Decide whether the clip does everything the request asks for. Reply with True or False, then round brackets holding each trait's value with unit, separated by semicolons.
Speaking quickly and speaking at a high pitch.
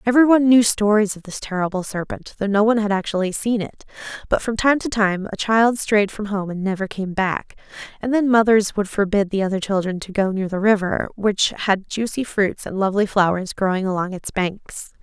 True (210 wpm; 205 Hz)